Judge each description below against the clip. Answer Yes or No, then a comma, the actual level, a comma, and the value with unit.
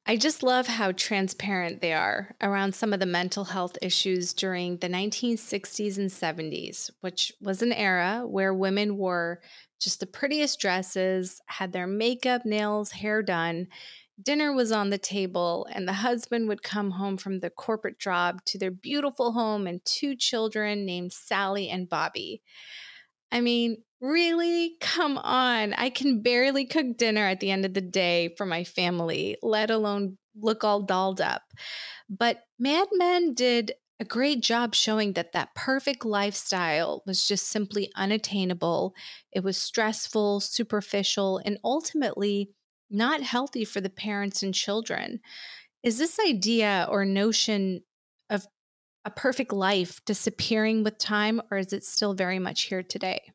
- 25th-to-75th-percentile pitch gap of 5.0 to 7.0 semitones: No, average, 3.7 semitones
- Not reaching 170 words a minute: Yes, average, 155 wpm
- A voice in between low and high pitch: No, high, 205 Hz